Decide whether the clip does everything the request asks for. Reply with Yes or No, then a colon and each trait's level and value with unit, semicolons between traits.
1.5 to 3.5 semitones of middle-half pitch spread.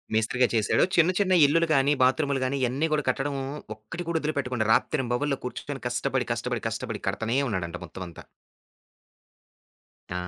No: average, 4.5 semitones